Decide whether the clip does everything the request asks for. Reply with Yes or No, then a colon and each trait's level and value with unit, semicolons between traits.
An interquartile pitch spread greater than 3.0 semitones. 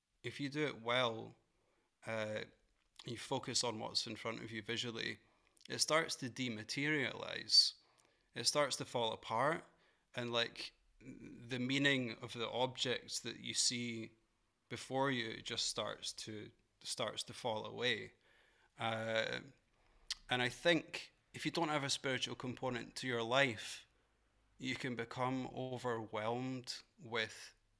No: narrow, 2.4 semitones